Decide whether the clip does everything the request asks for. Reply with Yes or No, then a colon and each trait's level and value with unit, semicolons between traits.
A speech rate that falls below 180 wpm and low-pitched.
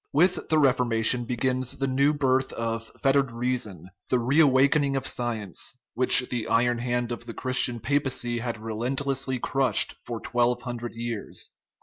Yes: average, 150 wpm; low, 125 Hz